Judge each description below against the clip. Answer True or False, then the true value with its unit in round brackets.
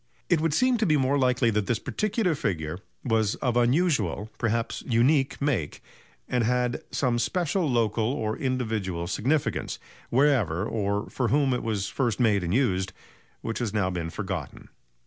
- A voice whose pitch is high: False (120 Hz)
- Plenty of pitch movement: False (4.9 semitones)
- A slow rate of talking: False (160 wpm)